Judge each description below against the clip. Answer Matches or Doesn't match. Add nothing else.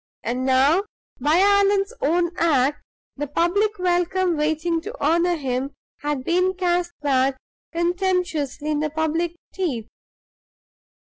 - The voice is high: Matches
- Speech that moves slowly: Matches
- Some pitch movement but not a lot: Matches